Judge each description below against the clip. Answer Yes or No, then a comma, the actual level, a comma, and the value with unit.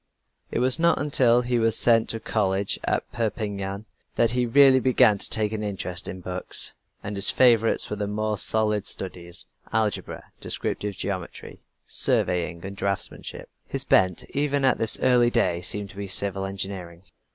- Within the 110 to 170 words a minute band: Yes, average, 165 wpm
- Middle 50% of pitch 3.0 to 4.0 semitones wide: Yes, average, 3.3 semitones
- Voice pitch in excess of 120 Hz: No, low, 105 Hz